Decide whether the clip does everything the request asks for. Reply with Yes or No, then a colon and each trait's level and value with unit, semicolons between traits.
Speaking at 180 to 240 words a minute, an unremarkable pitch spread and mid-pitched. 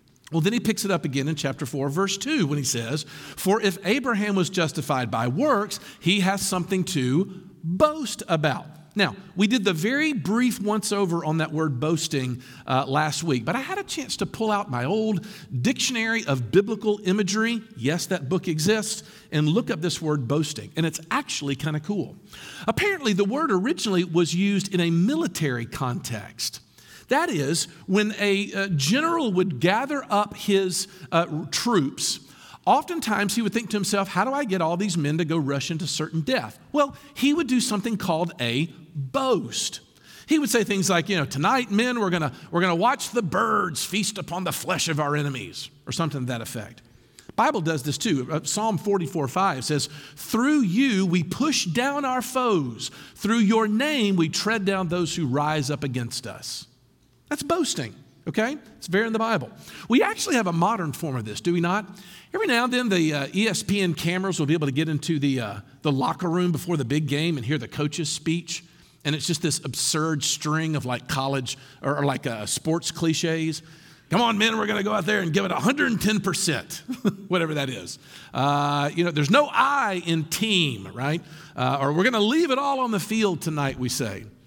No: average, 195 wpm; wide, 6.0 semitones; medium, 175 Hz